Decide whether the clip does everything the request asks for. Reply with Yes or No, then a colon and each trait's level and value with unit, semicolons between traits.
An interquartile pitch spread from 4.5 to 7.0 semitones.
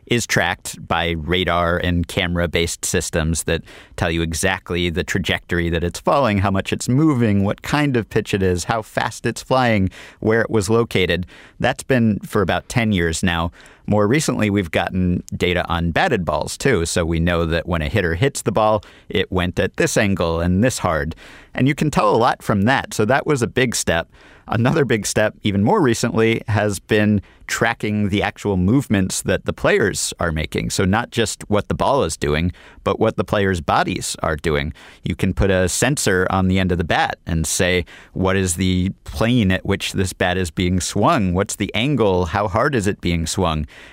No: average, 3.8 semitones